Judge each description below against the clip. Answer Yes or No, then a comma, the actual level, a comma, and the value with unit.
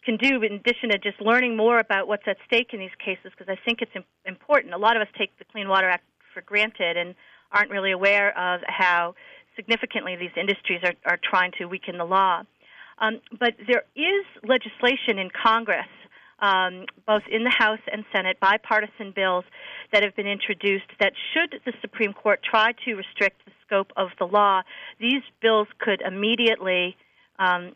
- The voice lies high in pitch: Yes, high, 205 Hz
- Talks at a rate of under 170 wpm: No, average, 185 wpm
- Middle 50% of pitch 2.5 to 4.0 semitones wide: Yes, average, 3.2 semitones